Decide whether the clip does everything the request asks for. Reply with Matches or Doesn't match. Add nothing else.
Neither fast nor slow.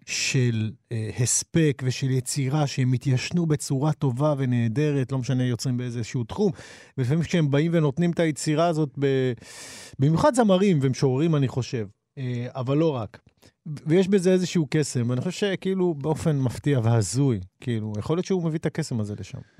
Doesn't match